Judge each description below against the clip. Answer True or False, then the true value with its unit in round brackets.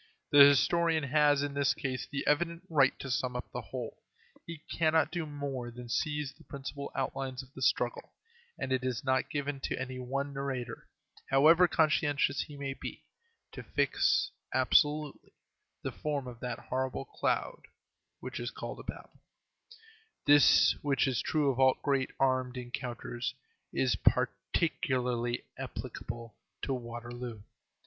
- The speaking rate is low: False (145 wpm)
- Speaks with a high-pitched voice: False (135 Hz)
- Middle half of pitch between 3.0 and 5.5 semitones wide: False (2.6 semitones)